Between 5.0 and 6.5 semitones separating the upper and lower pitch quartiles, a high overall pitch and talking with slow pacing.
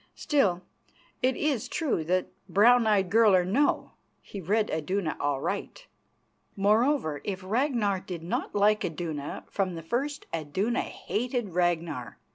Yes: wide, 5.4 semitones; high, 200 Hz; slow, 130 wpm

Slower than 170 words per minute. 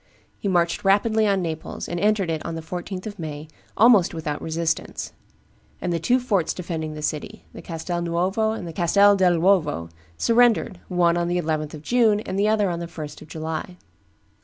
No: average, 190 wpm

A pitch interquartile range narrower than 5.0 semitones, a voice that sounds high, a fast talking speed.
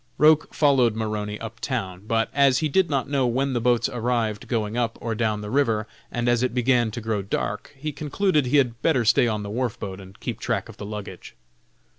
No: average, 3.9 semitones; low, 120 Hz; fast, 220 wpm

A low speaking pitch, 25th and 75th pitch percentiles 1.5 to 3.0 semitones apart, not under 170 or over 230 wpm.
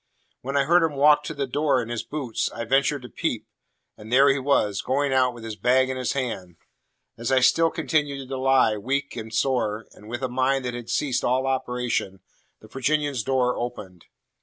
Yes: low, 130 Hz; narrow, 2.6 semitones; fast, 205 wpm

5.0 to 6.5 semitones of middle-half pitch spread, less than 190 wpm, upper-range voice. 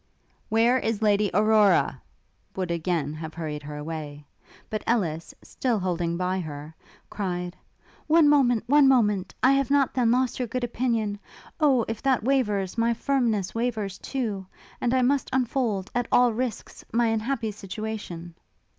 Yes: average, 5.3 semitones; average, 150 wpm; high, 220 Hz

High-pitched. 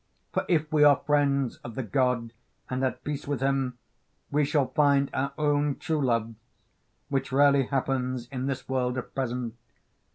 No: low, 135 Hz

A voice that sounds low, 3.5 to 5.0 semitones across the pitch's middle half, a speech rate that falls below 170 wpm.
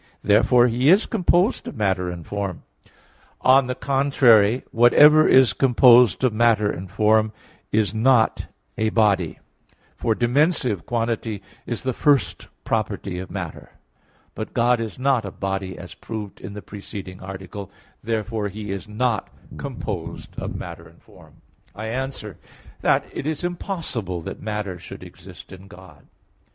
Yes: low, 110 Hz; average, 4.2 semitones; average, 140 wpm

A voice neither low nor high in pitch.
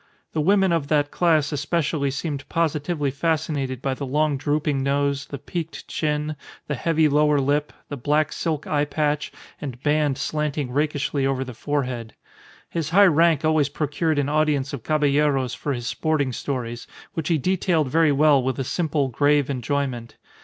Yes: medium, 145 Hz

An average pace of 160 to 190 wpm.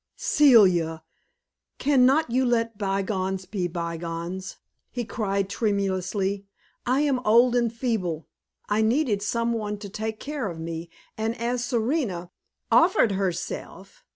No: average, 140 wpm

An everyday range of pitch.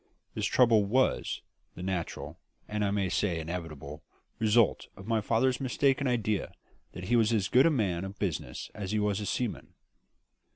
Yes: average, 4.0 semitones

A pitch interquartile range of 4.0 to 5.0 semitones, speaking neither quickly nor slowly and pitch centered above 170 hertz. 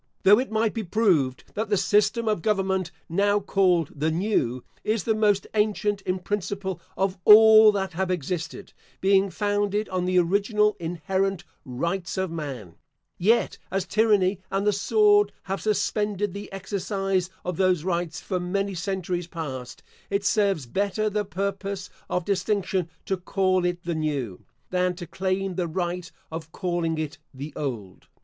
No: average, 2.9 semitones; average, 155 wpm; high, 190 Hz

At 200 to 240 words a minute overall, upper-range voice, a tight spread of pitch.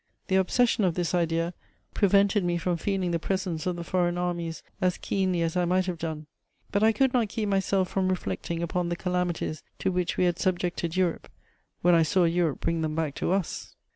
No: fast, 205 wpm; medium, 180 Hz; narrow, 2.0 semitones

